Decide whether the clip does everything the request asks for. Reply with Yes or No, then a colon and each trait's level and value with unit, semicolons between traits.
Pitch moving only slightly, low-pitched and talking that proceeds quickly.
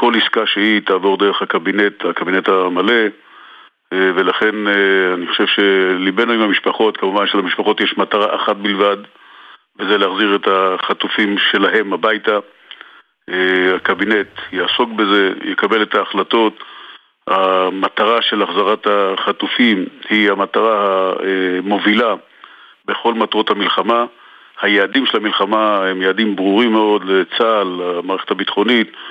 No: narrow, 2.0 semitones; low, 100 Hz; average, 105 wpm